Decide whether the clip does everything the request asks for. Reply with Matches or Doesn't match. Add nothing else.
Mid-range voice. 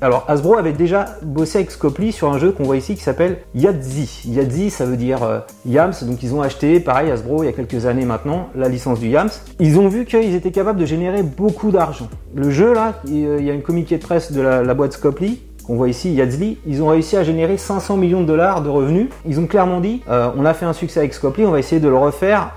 Matches